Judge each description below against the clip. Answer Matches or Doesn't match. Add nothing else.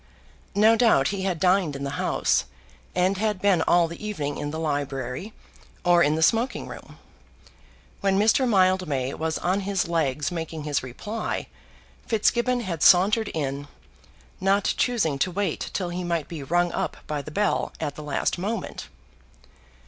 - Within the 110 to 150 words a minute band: Doesn't match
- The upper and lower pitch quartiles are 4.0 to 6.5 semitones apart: Matches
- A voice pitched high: Doesn't match